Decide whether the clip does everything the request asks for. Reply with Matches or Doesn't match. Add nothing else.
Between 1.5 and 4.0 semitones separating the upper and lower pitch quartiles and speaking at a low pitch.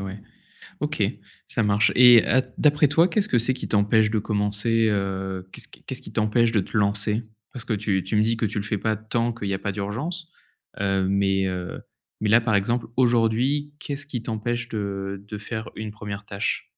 Matches